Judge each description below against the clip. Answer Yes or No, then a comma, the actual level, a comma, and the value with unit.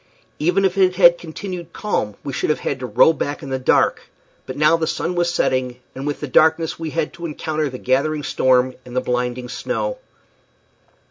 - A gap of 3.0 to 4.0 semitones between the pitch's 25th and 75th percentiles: No, average, 4.9 semitones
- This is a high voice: No, medium, 150 Hz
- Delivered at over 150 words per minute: Yes, average, 200 wpm